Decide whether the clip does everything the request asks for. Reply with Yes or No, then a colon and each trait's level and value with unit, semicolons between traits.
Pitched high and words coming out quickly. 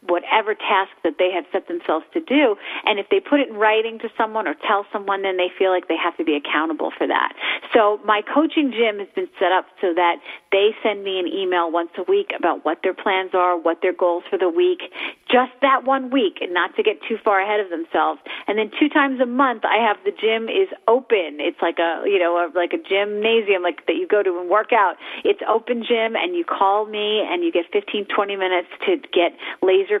Yes: high, 210 Hz; fast, 240 wpm